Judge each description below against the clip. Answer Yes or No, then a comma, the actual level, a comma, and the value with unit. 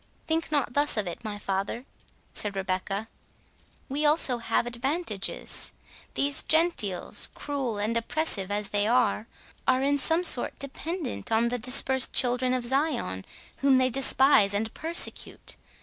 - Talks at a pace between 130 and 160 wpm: Yes, average, 140 wpm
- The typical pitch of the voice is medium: No, very high, 250 Hz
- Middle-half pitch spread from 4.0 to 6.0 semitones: Yes, average, 5.2 semitones